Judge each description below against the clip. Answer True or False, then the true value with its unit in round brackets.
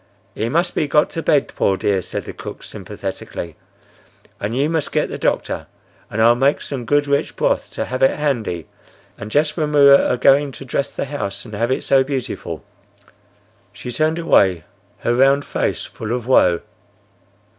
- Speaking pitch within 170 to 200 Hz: False (135 Hz)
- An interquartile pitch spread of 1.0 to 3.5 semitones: False (4.4 semitones)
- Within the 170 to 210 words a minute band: True (180 wpm)